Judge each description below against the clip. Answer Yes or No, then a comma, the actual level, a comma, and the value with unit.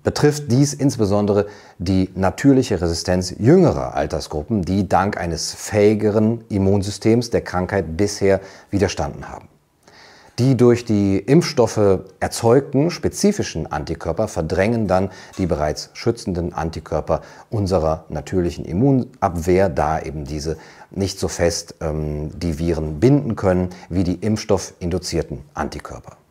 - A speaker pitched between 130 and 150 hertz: No, very low, 95 Hz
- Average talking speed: No, slow, 110 wpm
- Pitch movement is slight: No, average, 4.3 semitones